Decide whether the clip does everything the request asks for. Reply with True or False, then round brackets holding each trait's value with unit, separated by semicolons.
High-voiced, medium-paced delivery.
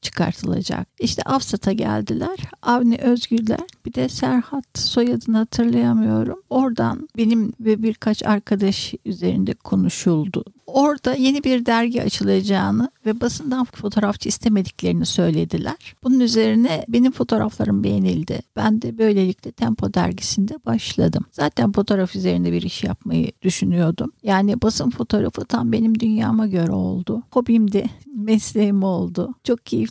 True (210 Hz; 120 wpm)